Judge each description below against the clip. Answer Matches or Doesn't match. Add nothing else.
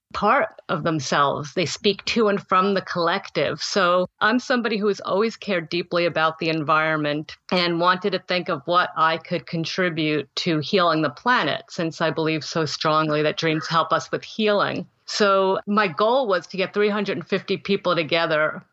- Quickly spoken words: Doesn't match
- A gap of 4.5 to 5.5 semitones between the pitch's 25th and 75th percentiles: Doesn't match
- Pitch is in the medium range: Matches